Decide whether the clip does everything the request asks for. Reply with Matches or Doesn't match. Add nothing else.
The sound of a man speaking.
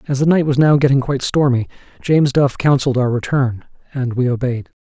Matches